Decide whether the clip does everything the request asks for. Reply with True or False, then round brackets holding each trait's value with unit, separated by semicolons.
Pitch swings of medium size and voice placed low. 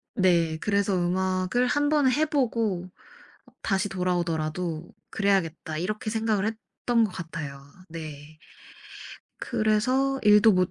False (4.7 semitones; 190 Hz)